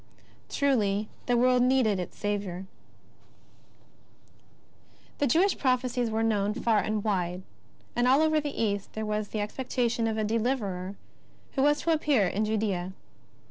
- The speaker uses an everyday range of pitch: Yes, average, 3.7 semitones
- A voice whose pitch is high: Yes, high, 220 Hz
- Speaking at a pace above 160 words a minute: No, average, 140 wpm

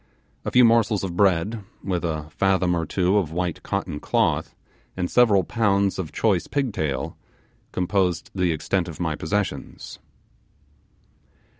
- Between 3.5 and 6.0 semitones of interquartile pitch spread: No, average, 3.1 semitones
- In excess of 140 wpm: No, slow, 135 wpm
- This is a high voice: No, very low, 95 Hz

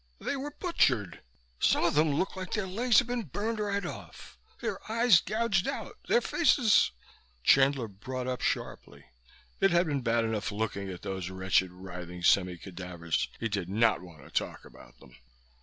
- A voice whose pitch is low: Yes, low, 120 Hz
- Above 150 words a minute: Yes, average, 175 wpm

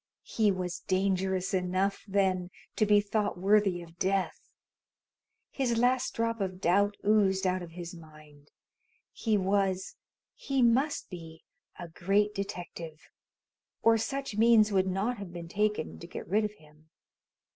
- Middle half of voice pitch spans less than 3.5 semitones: Yes, average, 3.0 semitones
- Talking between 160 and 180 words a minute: No, average, 145 wpm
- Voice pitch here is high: Yes, high, 195 Hz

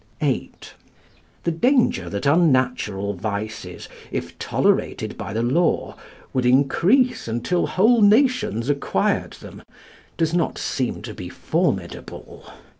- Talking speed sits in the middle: No, slow, 115 wpm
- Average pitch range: No, wide, 8.5 semitones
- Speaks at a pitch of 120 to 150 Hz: Yes, low, 135 Hz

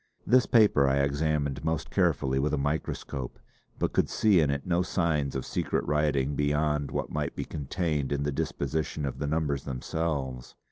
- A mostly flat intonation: Yes, narrow, 2.3 semitones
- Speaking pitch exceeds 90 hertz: No, very low, 75 Hz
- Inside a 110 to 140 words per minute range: No, average, 175 wpm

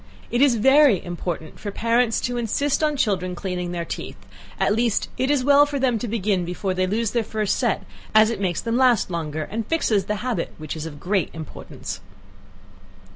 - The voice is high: Yes, high, 215 Hz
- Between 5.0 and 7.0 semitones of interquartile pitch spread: Yes, average, 5.3 semitones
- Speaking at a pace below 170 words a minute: No, average, 195 wpm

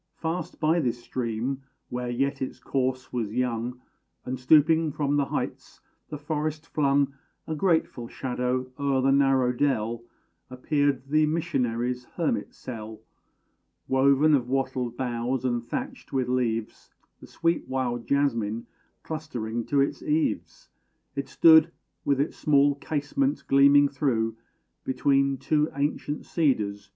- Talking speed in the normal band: No, slow, 130 wpm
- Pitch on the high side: No, low, 135 Hz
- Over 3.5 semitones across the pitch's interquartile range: No, average, 2.8 semitones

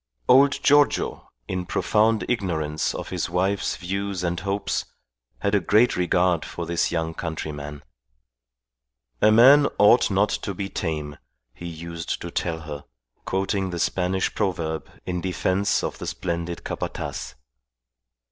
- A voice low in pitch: Yes, very low, 90 Hz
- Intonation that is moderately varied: Yes, average, 3.2 semitones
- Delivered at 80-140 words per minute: Yes, slow, 135 wpm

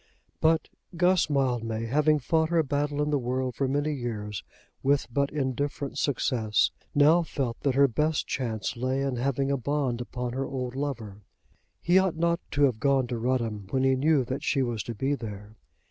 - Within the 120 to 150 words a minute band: No, average, 185 wpm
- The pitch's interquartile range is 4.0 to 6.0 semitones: No, average, 3.2 semitones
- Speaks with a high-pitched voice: No, low, 135 Hz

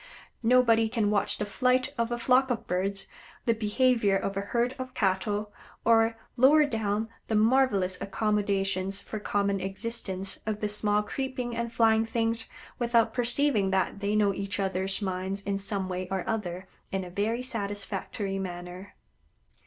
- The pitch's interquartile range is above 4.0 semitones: No, average, 3.1 semitones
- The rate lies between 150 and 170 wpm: Yes, average, 155 wpm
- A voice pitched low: No, high, 210 Hz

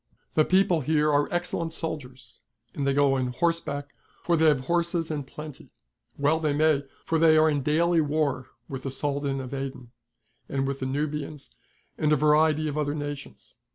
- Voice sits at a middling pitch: Yes, medium, 150 Hz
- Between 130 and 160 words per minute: No, average, 180 wpm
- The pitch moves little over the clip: Yes, narrow, 2.3 semitones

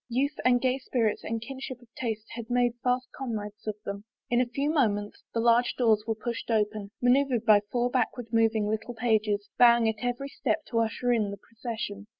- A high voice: Yes, high, 230 Hz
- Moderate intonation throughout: No, narrow, 2.3 semitones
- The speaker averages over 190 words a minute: Yes, fast, 205 wpm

